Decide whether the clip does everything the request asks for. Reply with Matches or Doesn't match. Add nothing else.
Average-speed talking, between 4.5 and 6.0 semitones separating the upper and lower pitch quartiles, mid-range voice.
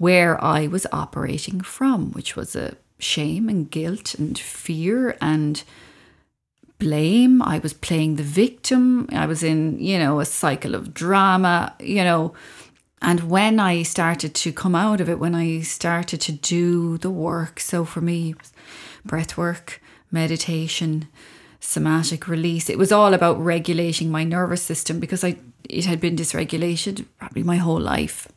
Doesn't match